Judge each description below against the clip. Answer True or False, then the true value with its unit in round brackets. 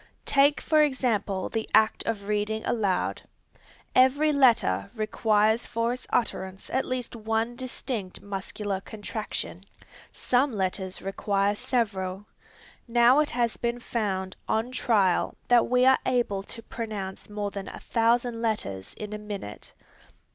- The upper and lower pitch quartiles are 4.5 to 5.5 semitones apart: False (3.4 semitones)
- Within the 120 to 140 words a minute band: True (135 wpm)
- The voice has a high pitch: True (220 Hz)